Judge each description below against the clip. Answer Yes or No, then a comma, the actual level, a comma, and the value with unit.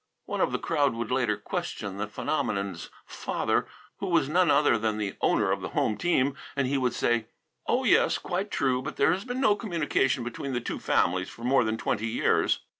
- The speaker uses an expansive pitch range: Yes, wide, 5.8 semitones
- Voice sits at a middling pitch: No, low, 130 Hz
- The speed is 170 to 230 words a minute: Yes, fast, 205 wpm